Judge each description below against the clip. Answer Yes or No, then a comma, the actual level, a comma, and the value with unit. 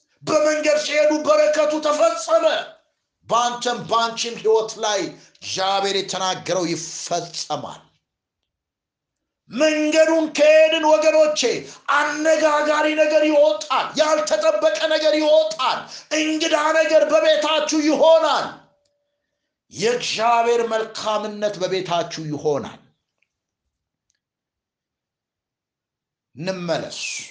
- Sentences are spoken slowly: Yes, slow, 65 wpm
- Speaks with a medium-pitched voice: No, very high, 300 Hz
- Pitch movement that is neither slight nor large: No, wide, 7.0 semitones